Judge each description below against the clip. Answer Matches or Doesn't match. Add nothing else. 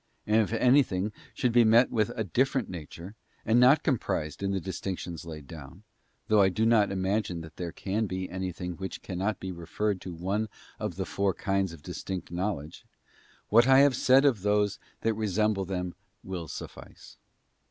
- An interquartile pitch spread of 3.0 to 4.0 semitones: Matches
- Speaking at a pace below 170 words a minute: Doesn't match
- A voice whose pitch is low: Matches